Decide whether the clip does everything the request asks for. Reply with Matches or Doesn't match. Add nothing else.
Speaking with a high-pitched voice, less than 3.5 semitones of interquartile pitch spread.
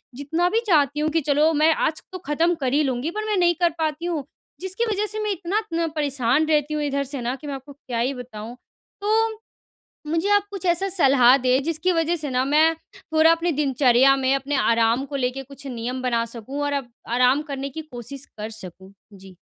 Doesn't match